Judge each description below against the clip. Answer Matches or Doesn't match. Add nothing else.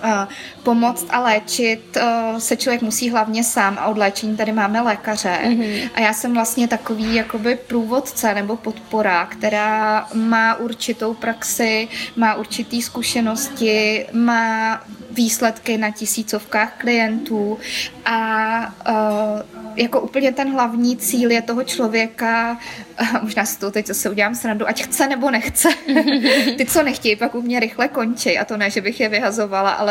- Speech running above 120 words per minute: Matches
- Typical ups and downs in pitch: Doesn't match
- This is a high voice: Matches